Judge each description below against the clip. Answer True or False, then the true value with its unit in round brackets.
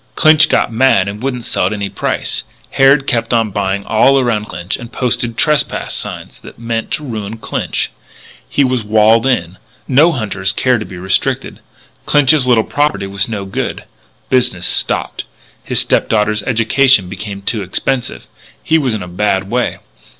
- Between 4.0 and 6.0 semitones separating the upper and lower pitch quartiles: True (4.5 semitones)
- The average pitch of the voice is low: True (115 Hz)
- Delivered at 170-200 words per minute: False (160 wpm)